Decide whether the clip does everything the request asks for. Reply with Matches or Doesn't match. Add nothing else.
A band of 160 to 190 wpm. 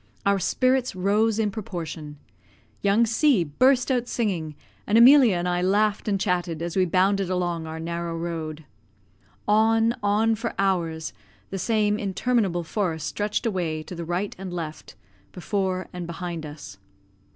Doesn't match